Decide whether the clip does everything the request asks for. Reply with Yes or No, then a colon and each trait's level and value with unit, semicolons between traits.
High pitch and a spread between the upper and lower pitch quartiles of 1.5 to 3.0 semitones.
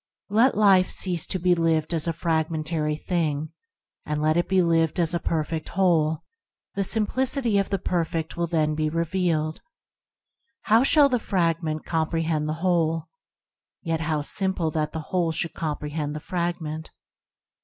No: medium, 165 Hz; narrow, 2.6 semitones